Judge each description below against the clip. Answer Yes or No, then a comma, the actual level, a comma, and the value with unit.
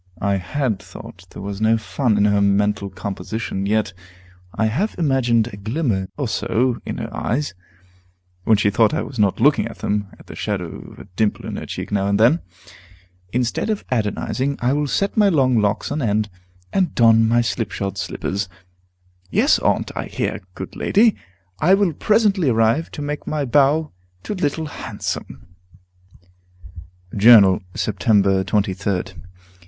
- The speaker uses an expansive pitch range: Yes, wide, 6.0 semitones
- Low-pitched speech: Yes, low, 110 Hz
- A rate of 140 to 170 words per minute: Yes, average, 160 wpm